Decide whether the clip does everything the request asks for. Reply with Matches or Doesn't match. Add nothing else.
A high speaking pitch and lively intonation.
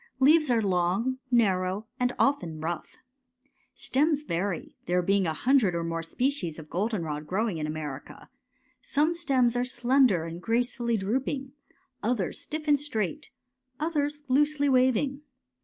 Matches